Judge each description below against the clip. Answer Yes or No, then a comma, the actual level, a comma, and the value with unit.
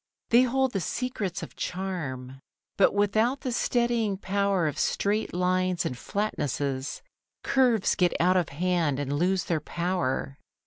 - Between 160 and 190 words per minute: No, average, 140 wpm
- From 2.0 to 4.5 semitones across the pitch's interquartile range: No, average, 5.1 semitones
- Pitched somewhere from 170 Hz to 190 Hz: Yes, medium, 185 Hz